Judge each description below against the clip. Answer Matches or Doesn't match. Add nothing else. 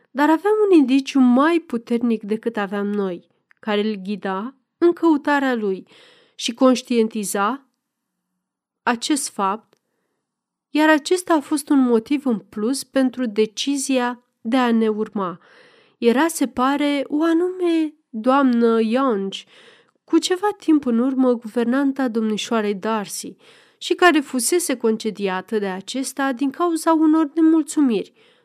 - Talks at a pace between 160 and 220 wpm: Doesn't match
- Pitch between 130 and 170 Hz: Doesn't match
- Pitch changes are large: Matches